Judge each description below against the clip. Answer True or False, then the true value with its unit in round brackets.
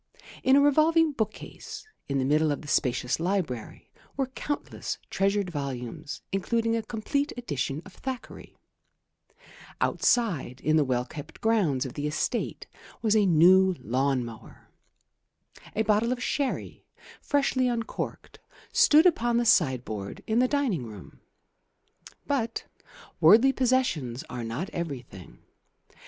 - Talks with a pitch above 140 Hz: True (190 Hz)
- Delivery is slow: True (130 wpm)